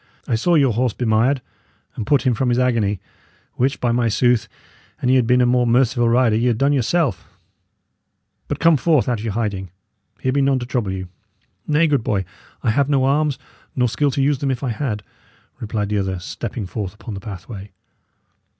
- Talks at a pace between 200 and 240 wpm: Yes, fast, 205 wpm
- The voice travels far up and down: No, average, 3.6 semitones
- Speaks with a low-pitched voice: Yes, low, 120 Hz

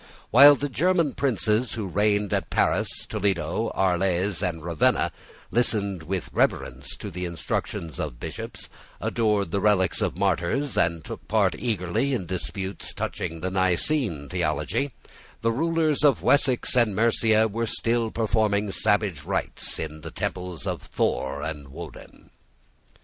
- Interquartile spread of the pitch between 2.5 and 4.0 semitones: No, average, 5.1 semitones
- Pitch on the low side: Yes, low, 100 Hz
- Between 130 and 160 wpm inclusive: Yes, average, 140 wpm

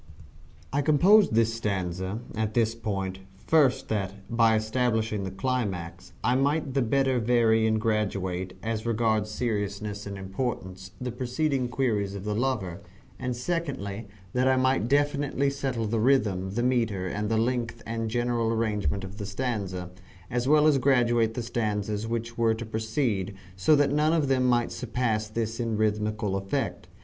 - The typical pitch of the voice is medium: No, low, 115 Hz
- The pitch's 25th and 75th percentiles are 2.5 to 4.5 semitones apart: Yes, average, 3.4 semitones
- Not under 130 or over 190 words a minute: Yes, average, 160 wpm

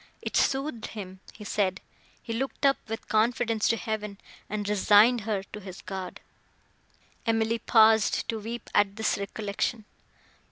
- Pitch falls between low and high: No, high, 220 Hz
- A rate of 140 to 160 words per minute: Yes, average, 145 wpm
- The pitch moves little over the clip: Yes, narrow, 1.9 semitones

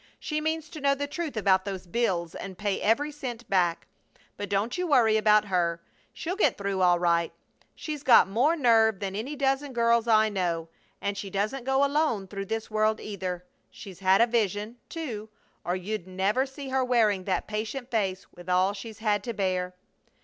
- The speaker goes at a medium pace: Yes, average, 190 wpm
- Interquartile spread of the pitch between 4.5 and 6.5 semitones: Yes, average, 4.9 semitones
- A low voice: No, high, 215 Hz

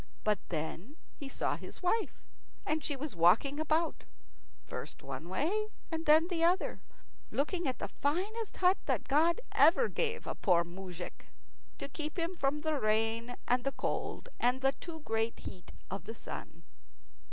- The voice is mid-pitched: No, very high, 285 Hz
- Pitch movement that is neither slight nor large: No, wide, 7.0 semitones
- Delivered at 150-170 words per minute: Yes, average, 165 wpm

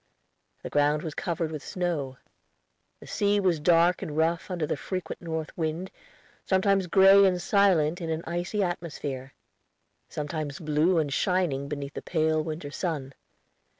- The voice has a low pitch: No, medium, 165 Hz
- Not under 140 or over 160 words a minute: Yes, average, 150 wpm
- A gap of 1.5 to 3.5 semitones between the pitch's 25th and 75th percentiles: Yes, average, 3.2 semitones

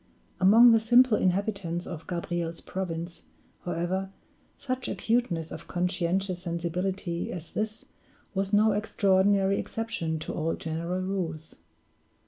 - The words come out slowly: Yes, slow, 110 wpm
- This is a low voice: No, medium, 185 Hz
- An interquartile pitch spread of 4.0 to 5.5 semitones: No, average, 3.2 semitones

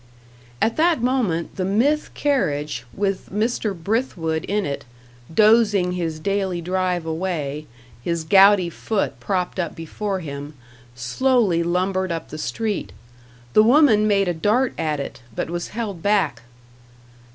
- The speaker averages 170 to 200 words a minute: No, slow, 135 wpm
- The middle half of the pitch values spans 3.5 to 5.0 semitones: Yes, average, 4.6 semitones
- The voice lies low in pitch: No, medium, 185 Hz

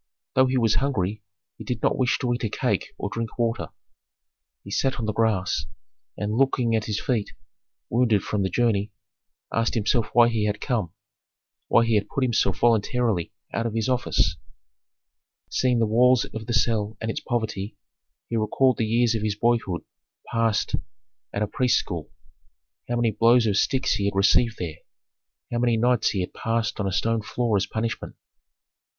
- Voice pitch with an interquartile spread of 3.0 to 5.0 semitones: No, narrow, 2.4 semitones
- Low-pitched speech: Yes, low, 115 Hz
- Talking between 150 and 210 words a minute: Yes, average, 180 wpm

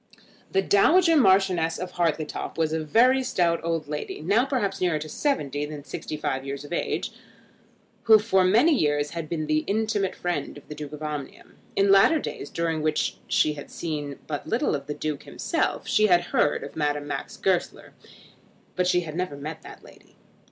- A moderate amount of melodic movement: Yes, average, 4.6 semitones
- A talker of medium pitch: Yes, medium, 165 Hz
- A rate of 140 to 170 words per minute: No, average, 185 wpm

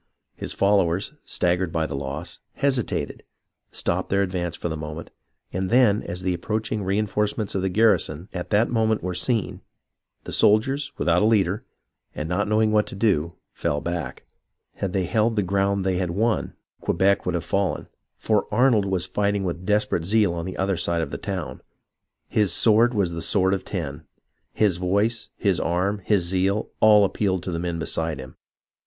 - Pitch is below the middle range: Yes, very low, 95 Hz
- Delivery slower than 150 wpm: No, average, 185 wpm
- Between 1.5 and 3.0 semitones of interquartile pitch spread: No, average, 3.5 semitones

